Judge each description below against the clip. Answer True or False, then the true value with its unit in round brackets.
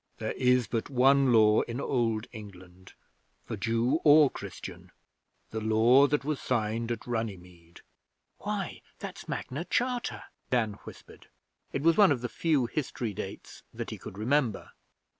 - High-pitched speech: False (120 Hz)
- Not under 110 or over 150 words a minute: True (145 wpm)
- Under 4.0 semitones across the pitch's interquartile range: False (4.3 semitones)